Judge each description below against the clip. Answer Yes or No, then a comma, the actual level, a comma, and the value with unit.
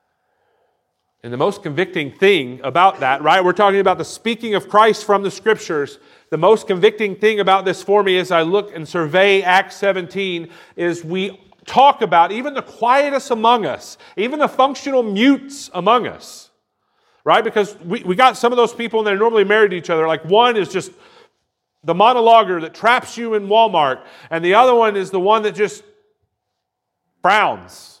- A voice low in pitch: No, high, 210 Hz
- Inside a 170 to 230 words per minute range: Yes, average, 180 wpm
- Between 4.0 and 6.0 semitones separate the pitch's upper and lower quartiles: Yes, average, 4.3 semitones